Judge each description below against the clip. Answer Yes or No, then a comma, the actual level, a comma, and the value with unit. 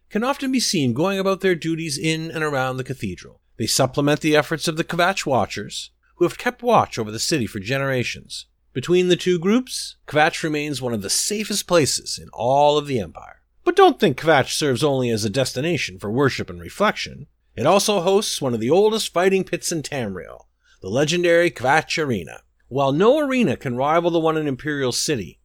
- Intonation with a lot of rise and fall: Yes, wide, 5.7 semitones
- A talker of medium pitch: Yes, medium, 155 Hz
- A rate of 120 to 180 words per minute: No, average, 200 wpm